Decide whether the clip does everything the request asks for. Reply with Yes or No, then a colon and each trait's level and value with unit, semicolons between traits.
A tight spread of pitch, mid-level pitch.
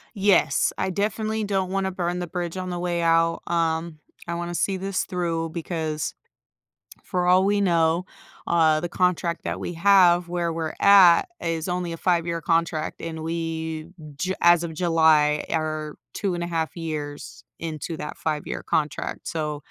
Yes: narrow, 1.9 semitones; medium, 170 Hz